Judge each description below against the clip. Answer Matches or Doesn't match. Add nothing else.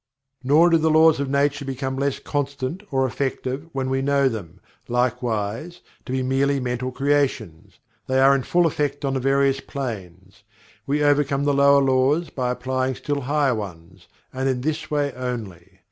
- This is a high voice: Doesn't match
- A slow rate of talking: Doesn't match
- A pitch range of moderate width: Doesn't match